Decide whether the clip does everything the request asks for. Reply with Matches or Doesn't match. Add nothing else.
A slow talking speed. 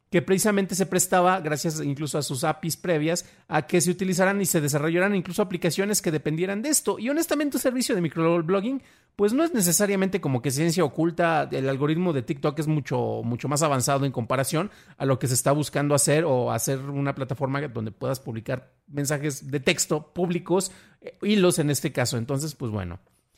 Doesn't match